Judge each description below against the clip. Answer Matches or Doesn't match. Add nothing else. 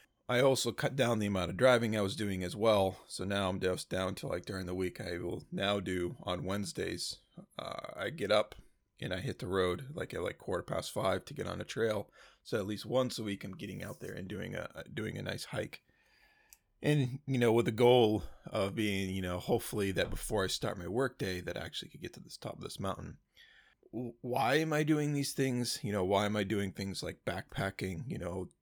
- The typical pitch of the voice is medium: Doesn't match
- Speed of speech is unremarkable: Doesn't match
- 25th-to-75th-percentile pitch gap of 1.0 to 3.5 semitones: Doesn't match